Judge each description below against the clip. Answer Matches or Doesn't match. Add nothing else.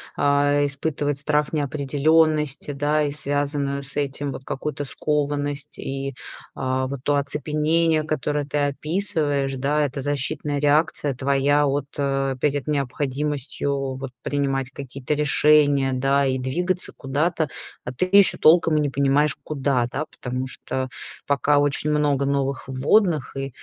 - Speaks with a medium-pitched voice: Matches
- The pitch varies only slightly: Matches